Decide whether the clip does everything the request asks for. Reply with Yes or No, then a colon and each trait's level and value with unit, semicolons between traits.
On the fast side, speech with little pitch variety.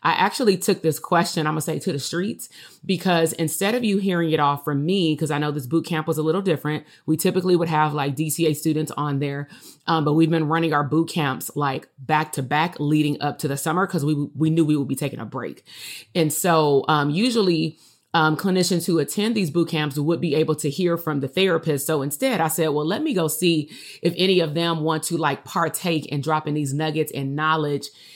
Yes: fast, 235 wpm; narrow, 2.2 semitones